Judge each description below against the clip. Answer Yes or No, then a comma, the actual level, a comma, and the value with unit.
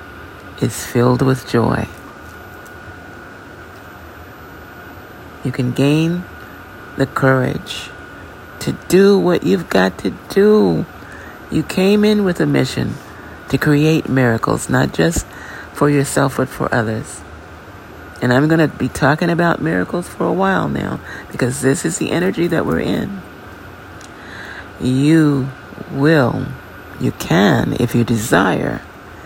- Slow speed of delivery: Yes, slow, 120 wpm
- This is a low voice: Yes, low, 120 Hz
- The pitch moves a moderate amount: No, wide, 7.3 semitones